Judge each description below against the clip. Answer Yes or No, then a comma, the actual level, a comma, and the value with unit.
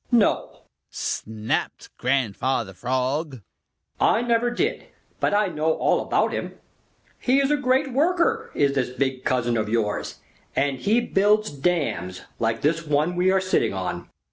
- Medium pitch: Yes, medium, 150 Hz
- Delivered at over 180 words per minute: No, average, 145 wpm